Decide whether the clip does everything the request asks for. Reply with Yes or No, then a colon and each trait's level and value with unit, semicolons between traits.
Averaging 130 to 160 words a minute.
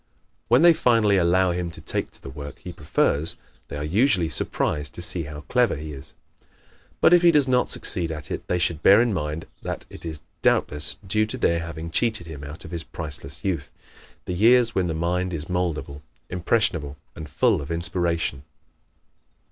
No: average, 190 wpm